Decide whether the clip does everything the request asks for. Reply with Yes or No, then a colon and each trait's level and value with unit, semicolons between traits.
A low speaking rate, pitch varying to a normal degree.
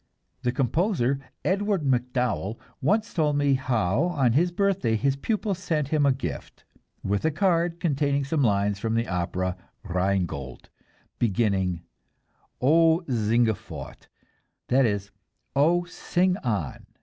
No: slow, 125 wpm; wide, 7.7 semitones